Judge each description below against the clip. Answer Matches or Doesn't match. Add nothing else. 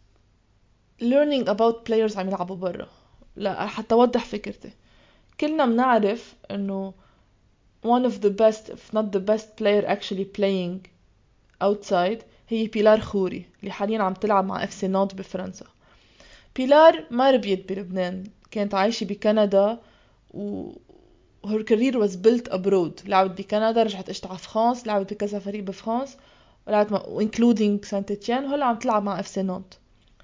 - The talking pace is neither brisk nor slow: Doesn't match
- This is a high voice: Matches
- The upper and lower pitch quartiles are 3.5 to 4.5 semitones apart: Doesn't match